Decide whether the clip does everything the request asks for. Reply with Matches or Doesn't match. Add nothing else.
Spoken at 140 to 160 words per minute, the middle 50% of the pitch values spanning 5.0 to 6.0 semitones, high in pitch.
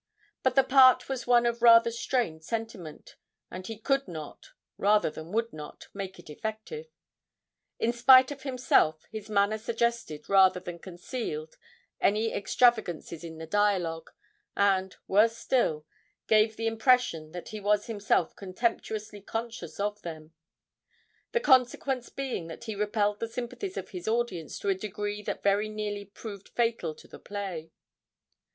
Doesn't match